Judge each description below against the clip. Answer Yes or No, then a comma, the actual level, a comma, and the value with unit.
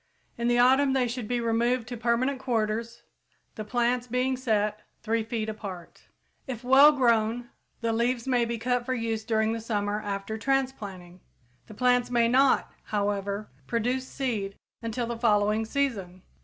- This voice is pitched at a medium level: No, high, 230 Hz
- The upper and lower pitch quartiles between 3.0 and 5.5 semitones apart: No, narrow, 2.6 semitones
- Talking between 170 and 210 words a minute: No, average, 155 wpm